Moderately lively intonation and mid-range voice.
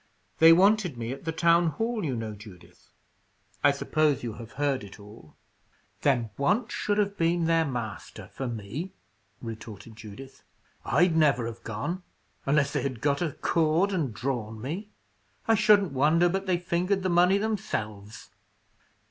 No: wide, 7.3 semitones; medium, 145 Hz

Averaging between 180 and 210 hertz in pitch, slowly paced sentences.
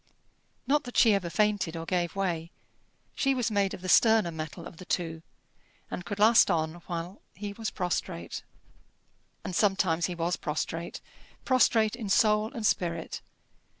No: medium, 185 Hz; average, 155 wpm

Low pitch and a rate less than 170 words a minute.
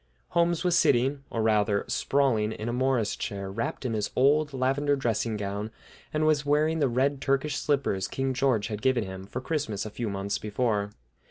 No: low, 125 Hz; average, 185 wpm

